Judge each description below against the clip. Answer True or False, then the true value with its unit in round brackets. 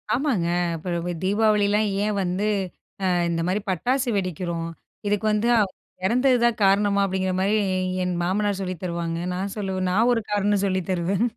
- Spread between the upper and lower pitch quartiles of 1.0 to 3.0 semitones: True (2.6 semitones)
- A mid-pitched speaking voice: False (195 Hz)